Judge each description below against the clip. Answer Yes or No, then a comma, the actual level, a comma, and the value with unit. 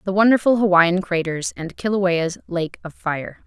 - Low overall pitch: No, medium, 185 Hz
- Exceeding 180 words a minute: No, average, 155 wpm